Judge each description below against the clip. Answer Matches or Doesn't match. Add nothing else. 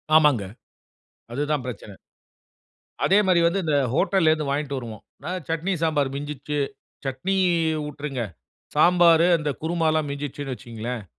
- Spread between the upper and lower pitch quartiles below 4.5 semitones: Matches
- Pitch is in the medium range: Matches